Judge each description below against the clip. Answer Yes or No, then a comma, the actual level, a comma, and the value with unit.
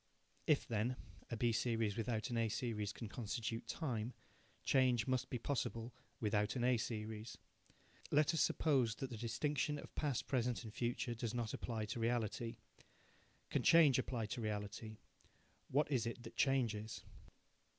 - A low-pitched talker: Yes, low, 115 Hz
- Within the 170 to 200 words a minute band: No, average, 155 wpm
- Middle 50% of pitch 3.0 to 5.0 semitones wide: No, narrow, 2.5 semitones